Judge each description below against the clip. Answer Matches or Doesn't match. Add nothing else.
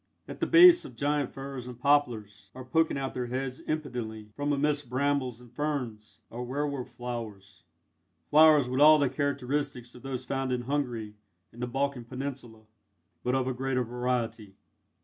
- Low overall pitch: Matches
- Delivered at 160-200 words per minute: Matches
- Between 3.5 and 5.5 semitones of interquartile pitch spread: Doesn't match